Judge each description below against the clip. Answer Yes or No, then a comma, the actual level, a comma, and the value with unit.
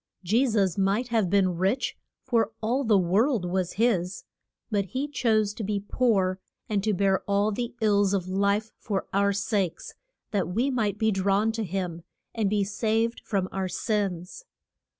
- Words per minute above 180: No, average, 170 wpm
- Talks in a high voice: Yes, high, 205 Hz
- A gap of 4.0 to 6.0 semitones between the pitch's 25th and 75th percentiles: No, narrow, 2.6 semitones